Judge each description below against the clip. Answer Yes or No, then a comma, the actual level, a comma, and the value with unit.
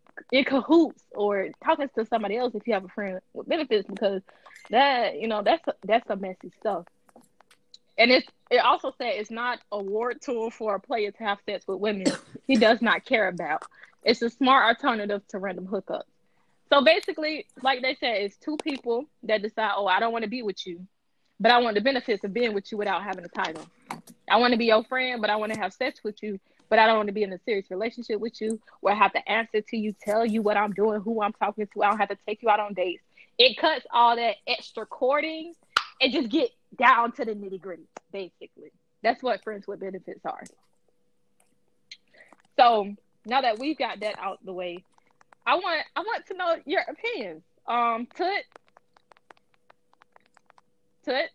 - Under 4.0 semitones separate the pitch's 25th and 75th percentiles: No, average, 4.3 semitones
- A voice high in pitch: Yes, high, 225 Hz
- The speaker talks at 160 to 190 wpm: No, fast, 205 wpm